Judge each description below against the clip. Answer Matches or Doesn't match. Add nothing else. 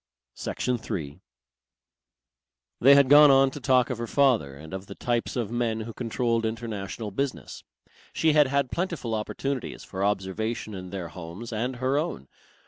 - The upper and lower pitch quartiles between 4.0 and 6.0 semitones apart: Matches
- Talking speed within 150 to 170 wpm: Matches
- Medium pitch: Doesn't match